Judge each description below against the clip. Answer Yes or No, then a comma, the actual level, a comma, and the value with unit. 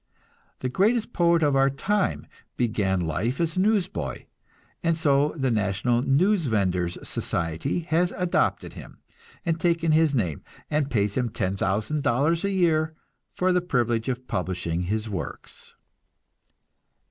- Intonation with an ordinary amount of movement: No, wide, 8.2 semitones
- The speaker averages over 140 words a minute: No, slow, 135 wpm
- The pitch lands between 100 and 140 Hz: Yes, low, 135 Hz